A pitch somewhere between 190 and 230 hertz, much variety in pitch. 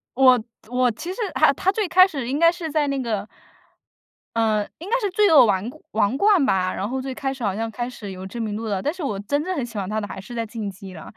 No: high, 245 Hz; wide, 6.6 semitones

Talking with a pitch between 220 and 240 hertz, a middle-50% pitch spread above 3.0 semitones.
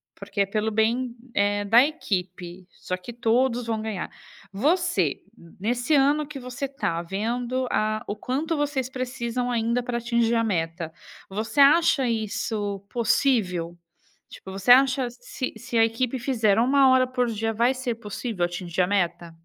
Yes: high, 230 Hz; average, 4.0 semitones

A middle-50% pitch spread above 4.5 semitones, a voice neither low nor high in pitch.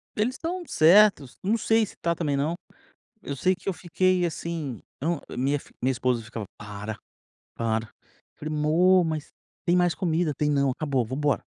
Yes: average, 5.3 semitones; medium, 155 Hz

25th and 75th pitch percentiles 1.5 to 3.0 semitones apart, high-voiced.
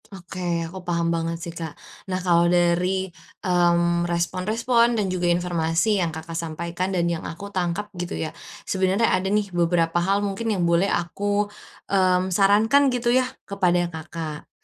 No: narrow, 2.6 semitones; medium, 180 Hz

